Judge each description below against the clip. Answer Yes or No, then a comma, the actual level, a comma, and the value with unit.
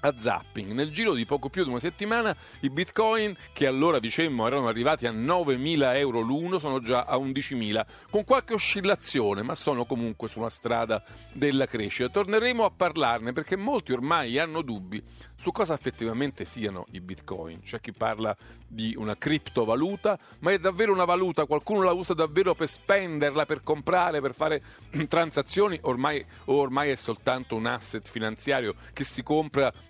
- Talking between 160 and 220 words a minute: Yes, average, 165 wpm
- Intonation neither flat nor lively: No, wide, 7.3 semitones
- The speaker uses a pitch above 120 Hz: Yes, medium, 140 Hz